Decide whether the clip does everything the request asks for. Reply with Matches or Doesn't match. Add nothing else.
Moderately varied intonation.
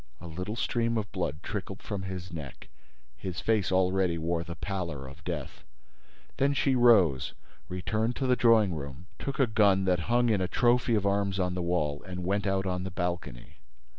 Matches